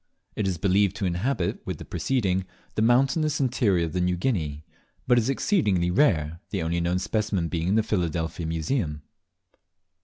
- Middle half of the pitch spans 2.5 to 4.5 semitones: No, average, 5.2 semitones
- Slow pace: No, average, 160 wpm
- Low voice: Yes, very low, 95 Hz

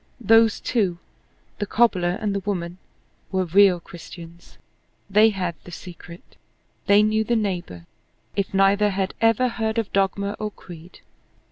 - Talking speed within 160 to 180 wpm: No, average, 140 wpm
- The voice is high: Yes, high, 195 Hz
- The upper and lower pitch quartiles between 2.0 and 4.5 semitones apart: Yes, average, 3.2 semitones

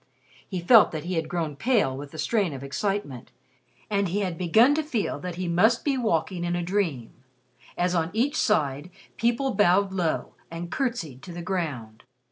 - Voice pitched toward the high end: No, medium, 180 Hz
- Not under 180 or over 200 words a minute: Yes, average, 185 wpm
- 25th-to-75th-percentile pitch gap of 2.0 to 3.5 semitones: No, average, 4.8 semitones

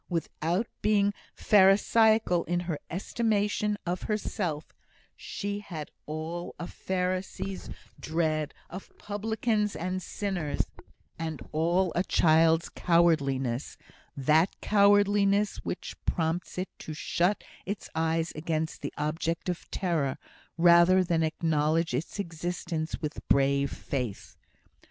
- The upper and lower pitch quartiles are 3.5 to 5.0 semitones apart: Yes, average, 3.8 semitones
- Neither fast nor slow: No, slow, 110 wpm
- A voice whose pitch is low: No, medium, 170 Hz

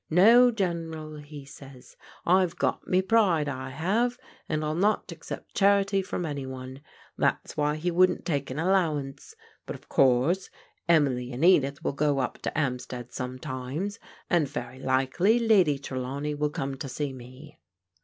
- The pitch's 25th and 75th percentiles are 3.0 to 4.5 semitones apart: No, wide, 5.4 semitones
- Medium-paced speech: Yes, average, 165 wpm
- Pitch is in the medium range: Yes, medium, 150 Hz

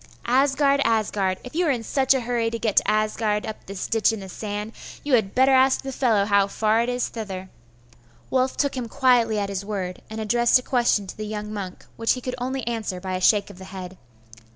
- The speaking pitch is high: Yes, high, 220 Hz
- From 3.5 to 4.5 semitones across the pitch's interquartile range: Yes, average, 3.8 semitones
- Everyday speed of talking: No, fast, 230 wpm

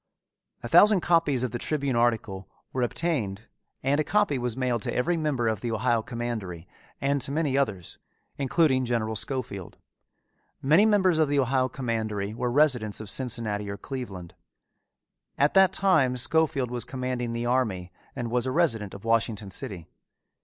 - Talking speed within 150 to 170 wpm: Yes, average, 160 wpm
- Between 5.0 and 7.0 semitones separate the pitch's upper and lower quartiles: No, average, 4.2 semitones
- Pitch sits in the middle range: No, low, 125 Hz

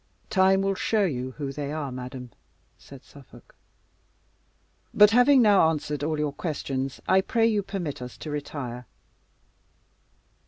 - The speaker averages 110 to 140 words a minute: Yes, slow, 135 wpm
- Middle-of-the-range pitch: Yes, medium, 150 Hz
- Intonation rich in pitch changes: Yes, wide, 6.2 semitones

